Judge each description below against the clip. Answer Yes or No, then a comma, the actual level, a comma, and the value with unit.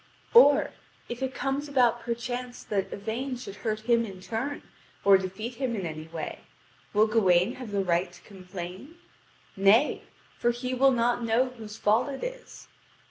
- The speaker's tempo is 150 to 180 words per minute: Yes, average, 165 wpm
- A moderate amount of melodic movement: Yes, average, 4.4 semitones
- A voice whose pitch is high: Yes, high, 230 Hz